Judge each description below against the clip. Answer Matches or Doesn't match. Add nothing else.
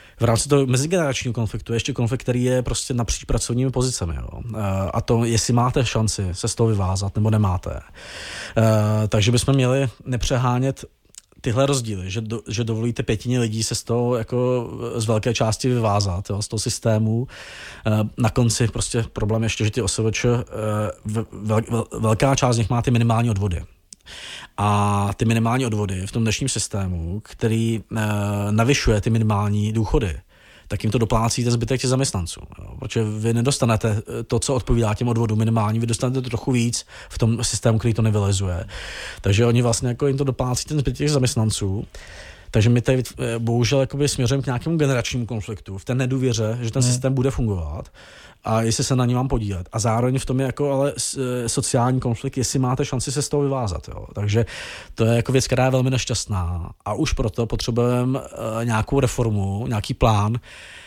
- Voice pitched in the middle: Doesn't match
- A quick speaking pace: Matches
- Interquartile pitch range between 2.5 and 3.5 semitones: Matches